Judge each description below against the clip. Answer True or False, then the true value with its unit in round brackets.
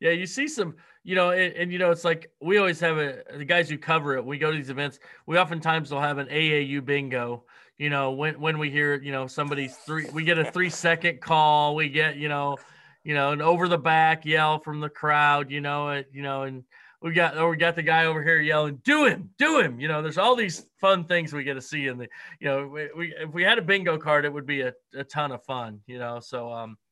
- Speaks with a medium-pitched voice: True (155 Hz)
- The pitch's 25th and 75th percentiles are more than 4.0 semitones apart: False (2.9 semitones)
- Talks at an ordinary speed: False (260 wpm)